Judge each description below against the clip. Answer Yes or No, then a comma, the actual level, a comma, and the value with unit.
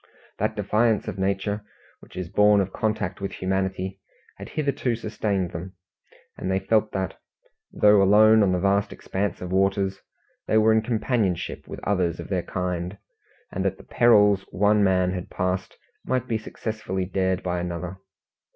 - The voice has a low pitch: Yes, very low, 95 Hz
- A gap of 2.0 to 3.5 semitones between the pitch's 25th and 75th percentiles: Yes, narrow, 2.5 semitones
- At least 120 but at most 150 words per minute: No, average, 160 wpm